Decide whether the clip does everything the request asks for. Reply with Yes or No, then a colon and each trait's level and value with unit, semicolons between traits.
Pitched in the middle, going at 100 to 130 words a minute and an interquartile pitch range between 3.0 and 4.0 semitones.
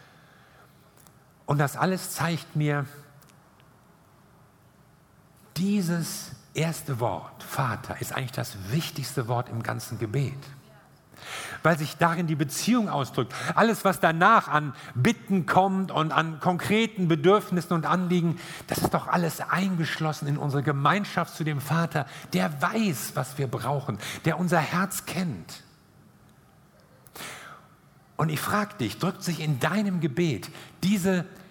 Yes: medium, 160 Hz; slow, 125 wpm; average, 3.7 semitones